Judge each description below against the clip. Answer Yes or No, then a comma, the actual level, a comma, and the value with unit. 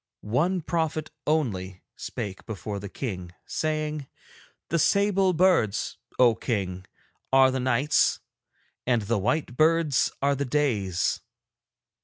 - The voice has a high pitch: No, low, 130 Hz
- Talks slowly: Yes, slow, 115 wpm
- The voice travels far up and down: Yes, wide, 7.1 semitones